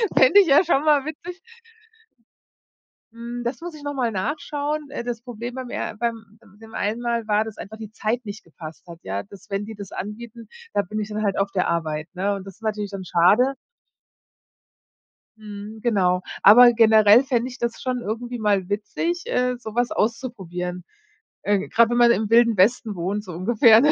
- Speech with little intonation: No, average, 3.2 semitones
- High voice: Yes, high, 220 Hz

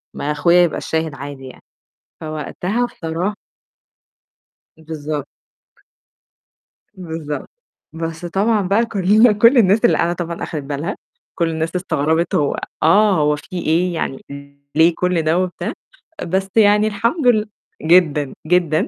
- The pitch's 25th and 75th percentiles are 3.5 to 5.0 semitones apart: Yes, average, 4.1 semitones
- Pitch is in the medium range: Yes, medium, 170 Hz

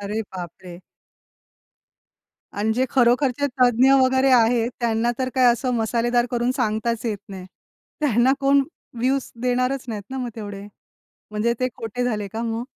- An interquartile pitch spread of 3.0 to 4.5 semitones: No, narrow, 2.5 semitones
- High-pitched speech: Yes, high, 240 Hz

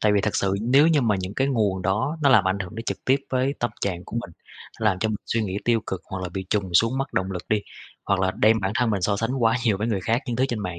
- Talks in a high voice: No, low, 105 Hz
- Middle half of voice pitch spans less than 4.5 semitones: Yes, average, 3.9 semitones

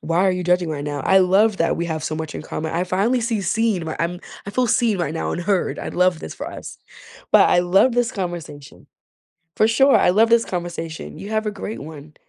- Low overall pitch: No, medium, 180 Hz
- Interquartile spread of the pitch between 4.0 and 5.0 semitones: Yes, average, 4.6 semitones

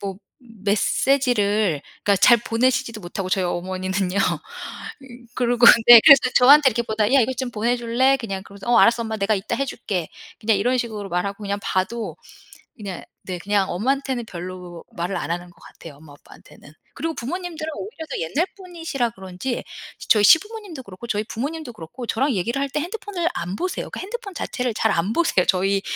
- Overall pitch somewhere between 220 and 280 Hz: Yes, high, 225 Hz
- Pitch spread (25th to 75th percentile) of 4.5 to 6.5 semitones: Yes, wide, 5.6 semitones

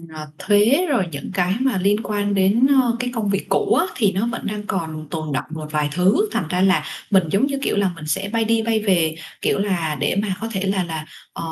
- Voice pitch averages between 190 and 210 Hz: Yes, high, 195 Hz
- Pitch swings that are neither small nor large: Yes, average, 4.6 semitones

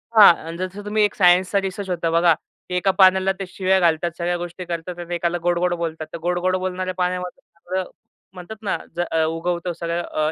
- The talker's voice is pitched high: No, medium, 180 Hz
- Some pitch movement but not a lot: No, narrow, 1.5 semitones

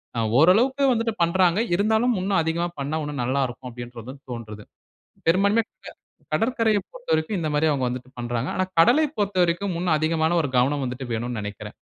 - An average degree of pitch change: No, wide, 7.9 semitones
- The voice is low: No, medium, 160 Hz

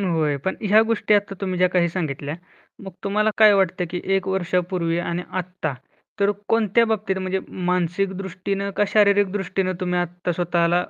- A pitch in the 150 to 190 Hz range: Yes, medium, 185 Hz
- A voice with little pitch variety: Yes, narrow, 2.1 semitones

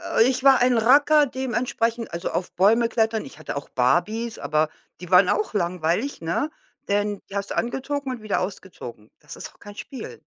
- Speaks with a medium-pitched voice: No, high, 220 Hz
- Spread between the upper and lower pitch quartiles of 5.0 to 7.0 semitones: Yes, wide, 5.6 semitones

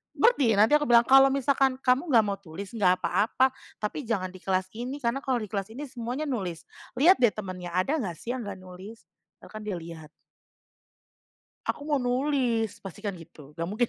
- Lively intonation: Yes, wide, 5.8 semitones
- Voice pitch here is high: Yes, high, 225 Hz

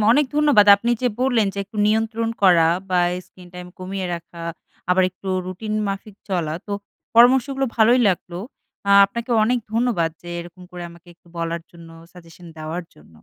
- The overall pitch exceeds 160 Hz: Yes, high, 190 Hz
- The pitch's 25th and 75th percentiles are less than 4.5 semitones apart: No, average, 4.8 semitones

